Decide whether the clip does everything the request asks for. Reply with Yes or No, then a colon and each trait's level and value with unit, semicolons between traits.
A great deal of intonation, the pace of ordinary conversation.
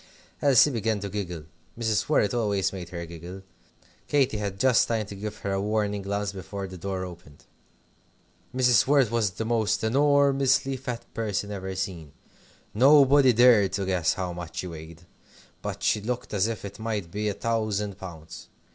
No: average, 3.6 semitones; average, 170 wpm